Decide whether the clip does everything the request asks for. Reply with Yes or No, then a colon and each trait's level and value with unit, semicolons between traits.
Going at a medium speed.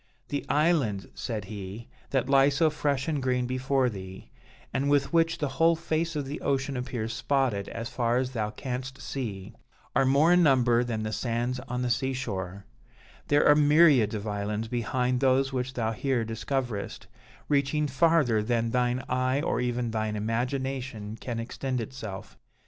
Yes: average, 165 wpm